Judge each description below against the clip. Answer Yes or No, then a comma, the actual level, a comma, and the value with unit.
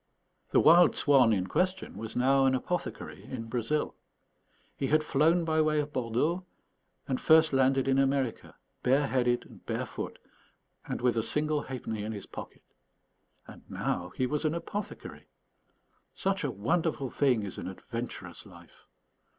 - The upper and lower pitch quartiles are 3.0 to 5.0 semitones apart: Yes, average, 4.4 semitones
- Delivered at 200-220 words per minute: No, average, 150 wpm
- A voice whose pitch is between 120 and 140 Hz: Yes, low, 135 Hz